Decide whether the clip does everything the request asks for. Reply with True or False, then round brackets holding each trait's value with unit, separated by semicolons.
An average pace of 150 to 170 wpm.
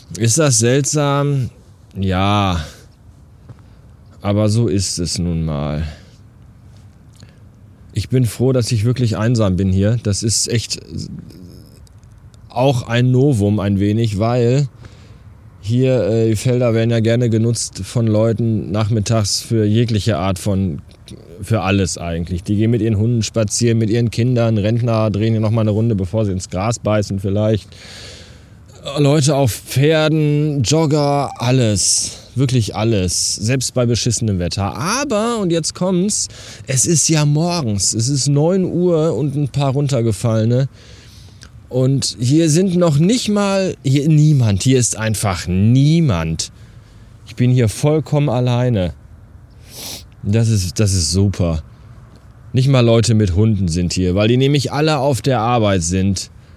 False (140 wpm)